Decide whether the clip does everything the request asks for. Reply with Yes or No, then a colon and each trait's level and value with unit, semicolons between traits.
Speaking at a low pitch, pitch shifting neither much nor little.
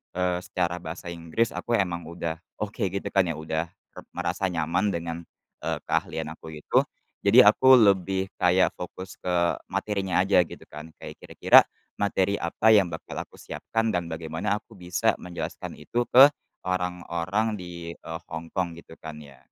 Yes: very low, 90 Hz; average, 3.1 semitones